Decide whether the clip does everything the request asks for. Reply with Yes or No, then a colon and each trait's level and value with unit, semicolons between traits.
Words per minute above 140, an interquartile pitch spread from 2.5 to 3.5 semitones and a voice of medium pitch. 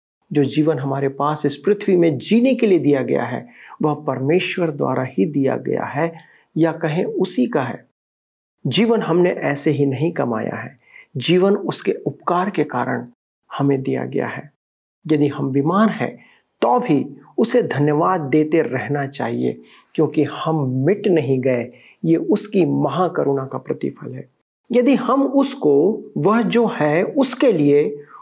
No: average, 150 wpm; average, 5.1 semitones; medium, 155 Hz